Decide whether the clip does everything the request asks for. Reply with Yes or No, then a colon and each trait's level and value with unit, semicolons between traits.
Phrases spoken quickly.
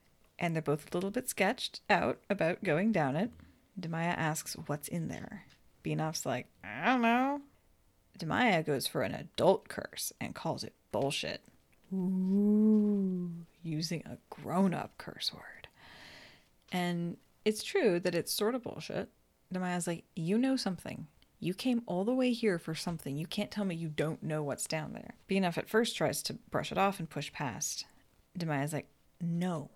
No: average, 170 wpm